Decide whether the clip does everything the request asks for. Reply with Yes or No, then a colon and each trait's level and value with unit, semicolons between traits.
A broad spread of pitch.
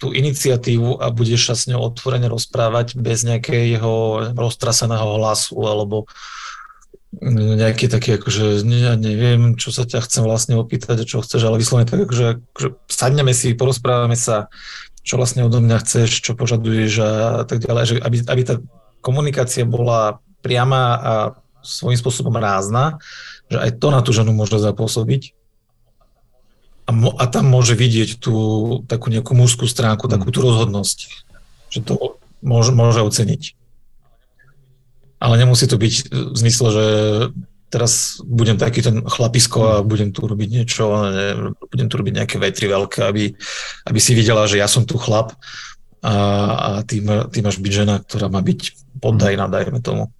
No: narrow, 2.4 semitones